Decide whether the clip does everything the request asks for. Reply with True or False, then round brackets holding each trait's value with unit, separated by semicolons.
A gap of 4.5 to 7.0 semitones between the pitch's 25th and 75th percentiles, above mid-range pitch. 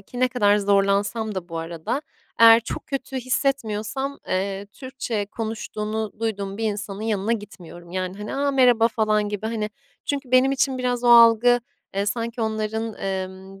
False (3.5 semitones; 220 Hz)